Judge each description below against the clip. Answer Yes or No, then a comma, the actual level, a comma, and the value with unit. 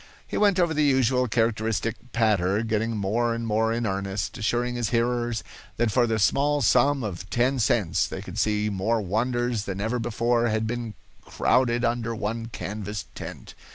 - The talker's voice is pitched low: Yes, low, 115 Hz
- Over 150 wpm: Yes, average, 170 wpm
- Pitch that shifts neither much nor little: No, narrow, 2.2 semitones